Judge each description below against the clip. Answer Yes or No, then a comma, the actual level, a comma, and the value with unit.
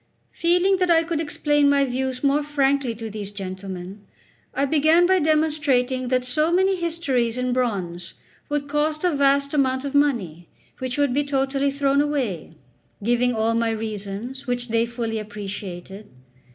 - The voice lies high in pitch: Yes, very high, 265 Hz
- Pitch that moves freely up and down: No, average, 4.6 semitones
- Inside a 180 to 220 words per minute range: No, average, 155 wpm